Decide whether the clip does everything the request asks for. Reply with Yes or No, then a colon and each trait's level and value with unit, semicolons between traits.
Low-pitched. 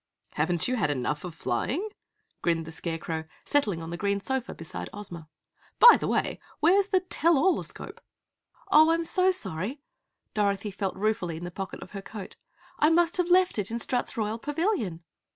No: high, 210 Hz